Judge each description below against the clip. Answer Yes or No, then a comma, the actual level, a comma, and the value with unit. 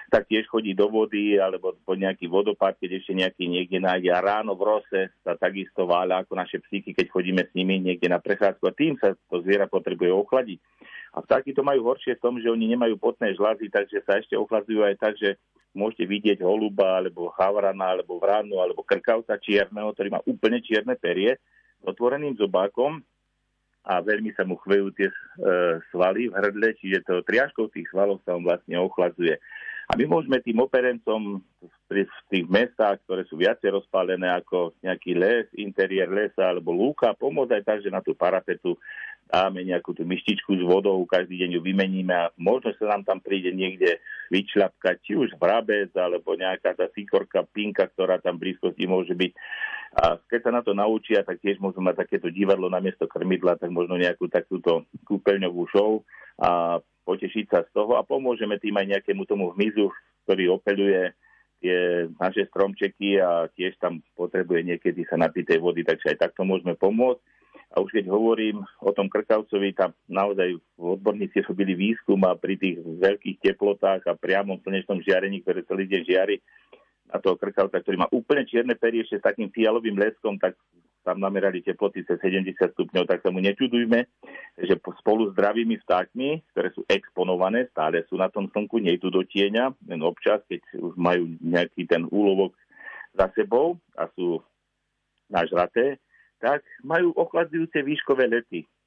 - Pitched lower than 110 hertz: Yes, low, 100 Hz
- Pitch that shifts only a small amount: No, average, 3.5 semitones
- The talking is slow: No, fast, 175 wpm